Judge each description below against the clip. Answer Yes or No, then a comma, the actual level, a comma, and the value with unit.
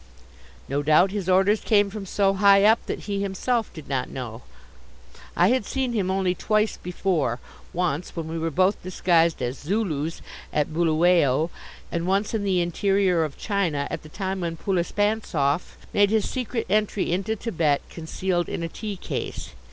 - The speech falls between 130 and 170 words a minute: Yes, average, 165 wpm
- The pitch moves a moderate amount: Yes, average, 3.9 semitones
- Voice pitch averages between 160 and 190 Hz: Yes, medium, 185 Hz